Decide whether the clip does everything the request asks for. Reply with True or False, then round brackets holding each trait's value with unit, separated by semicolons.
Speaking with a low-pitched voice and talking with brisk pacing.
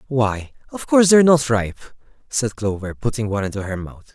False (115 Hz; 190 wpm)